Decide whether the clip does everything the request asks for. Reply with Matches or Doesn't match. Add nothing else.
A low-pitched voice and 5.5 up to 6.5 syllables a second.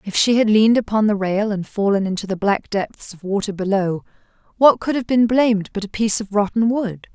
Doesn't match